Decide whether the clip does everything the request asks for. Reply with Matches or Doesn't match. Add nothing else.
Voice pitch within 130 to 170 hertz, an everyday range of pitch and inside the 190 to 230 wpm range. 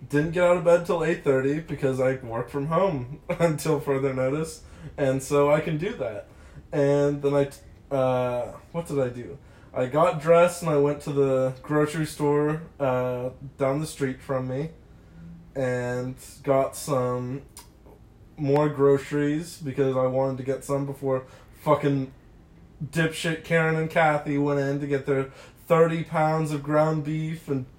Doesn't match